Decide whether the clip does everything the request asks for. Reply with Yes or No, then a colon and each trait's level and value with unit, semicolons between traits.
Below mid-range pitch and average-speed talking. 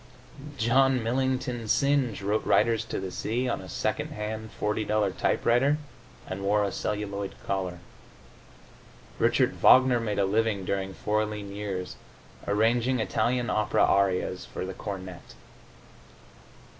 No: low, 105 Hz; slow, 125 wpm